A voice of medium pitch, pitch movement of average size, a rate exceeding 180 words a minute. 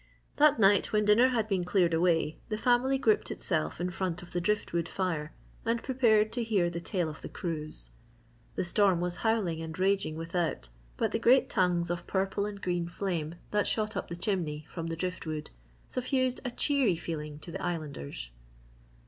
Yes: medium, 180 Hz; average, 4.5 semitones; average, 190 wpm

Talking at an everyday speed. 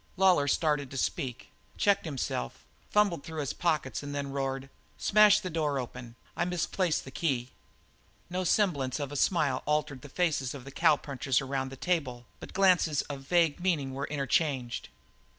Yes: average, 165 wpm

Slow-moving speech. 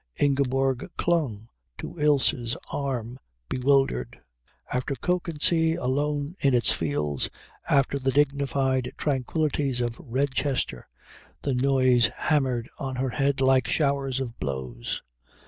Yes: slow, 110 wpm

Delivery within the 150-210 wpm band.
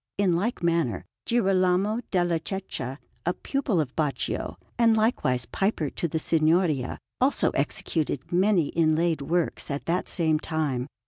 No: slow, 135 wpm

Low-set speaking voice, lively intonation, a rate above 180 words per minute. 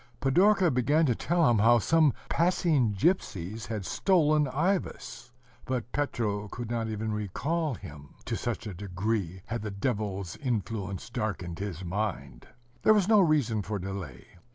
No: low, 115 Hz; wide, 6.8 semitones; average, 150 wpm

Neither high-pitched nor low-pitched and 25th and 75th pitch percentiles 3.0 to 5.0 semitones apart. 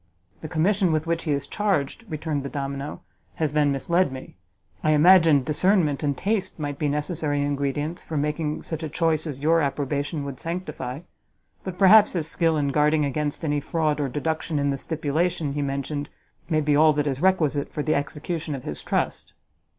No: medium, 150 Hz; narrow, 2.5 semitones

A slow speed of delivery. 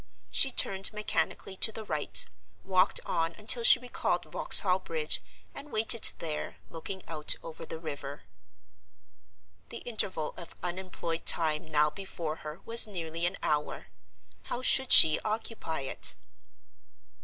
Yes: slow, 130 wpm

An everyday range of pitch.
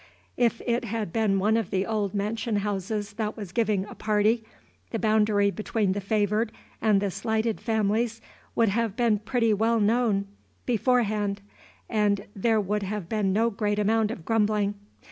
No: narrow, 1.8 semitones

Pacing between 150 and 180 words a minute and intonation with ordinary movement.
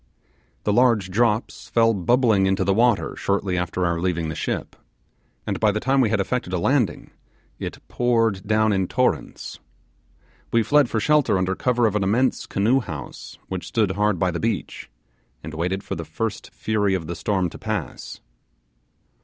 Yes: average, 175 wpm; average, 4.0 semitones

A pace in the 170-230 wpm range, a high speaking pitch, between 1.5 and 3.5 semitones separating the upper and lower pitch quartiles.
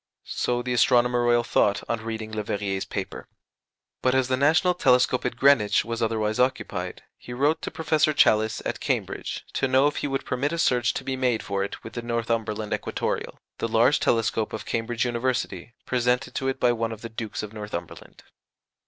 No: average, 190 wpm; low, 120 Hz; narrow, 2.6 semitones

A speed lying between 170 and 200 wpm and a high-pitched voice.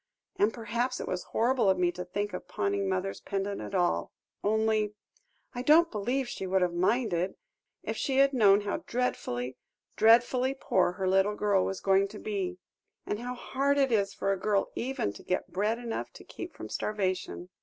Yes: average, 185 wpm; high, 205 Hz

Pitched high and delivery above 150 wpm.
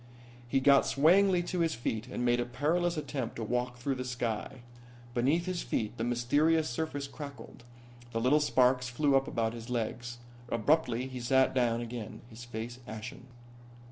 No: low, 125 Hz; average, 170 wpm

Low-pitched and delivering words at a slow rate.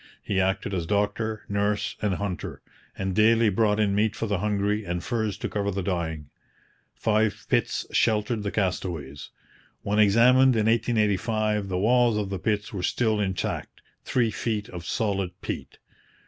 No: low, 105 Hz; average, 160 wpm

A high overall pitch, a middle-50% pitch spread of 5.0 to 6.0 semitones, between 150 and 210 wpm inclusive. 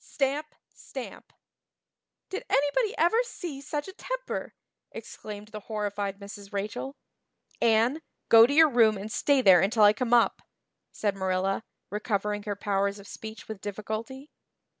No: high, 220 Hz; average, 5.3 semitones; average, 140 wpm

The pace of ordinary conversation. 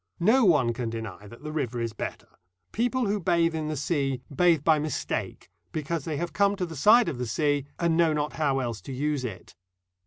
No: fast, 215 wpm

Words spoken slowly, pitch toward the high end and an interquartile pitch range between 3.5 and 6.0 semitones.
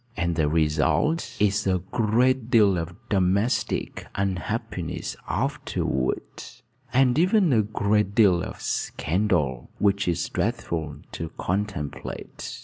No: slow, 110 wpm; low, 100 Hz; average, 4.7 semitones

